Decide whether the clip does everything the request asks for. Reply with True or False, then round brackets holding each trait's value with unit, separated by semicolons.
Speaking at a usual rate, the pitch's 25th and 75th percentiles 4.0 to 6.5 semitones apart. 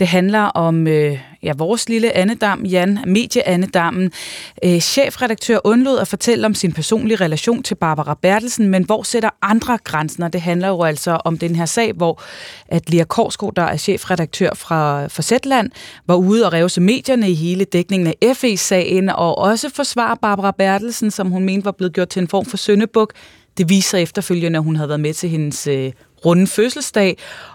True (180 wpm; 4.4 semitones)